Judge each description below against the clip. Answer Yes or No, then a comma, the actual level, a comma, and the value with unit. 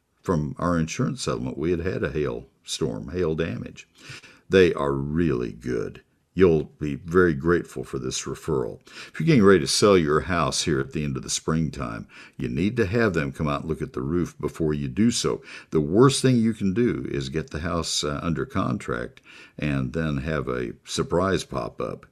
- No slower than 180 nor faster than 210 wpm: Yes, average, 200 wpm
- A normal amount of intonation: Yes, average, 3.7 semitones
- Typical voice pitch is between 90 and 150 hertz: No, very low, 80 Hz